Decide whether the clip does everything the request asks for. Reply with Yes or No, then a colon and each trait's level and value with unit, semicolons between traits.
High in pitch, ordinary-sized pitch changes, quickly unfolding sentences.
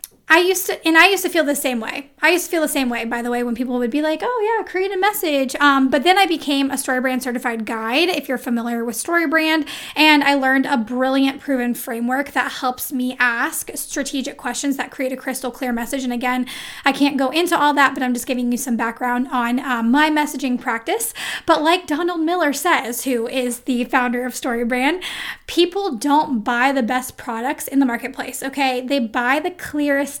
Yes: very high, 270 Hz; average, 3.5 semitones; fast, 215 wpm